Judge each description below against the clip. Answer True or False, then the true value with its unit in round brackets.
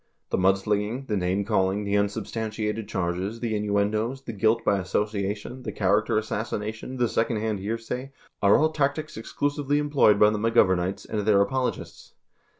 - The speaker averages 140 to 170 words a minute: True (155 wpm)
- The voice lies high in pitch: False (105 Hz)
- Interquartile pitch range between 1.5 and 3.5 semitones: True (2.6 semitones)